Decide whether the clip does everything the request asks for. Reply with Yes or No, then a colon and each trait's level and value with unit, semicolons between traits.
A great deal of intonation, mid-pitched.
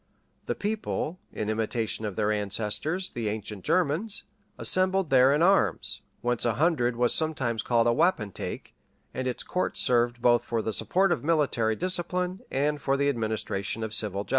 No: wide, 7.1 semitones; low, 125 Hz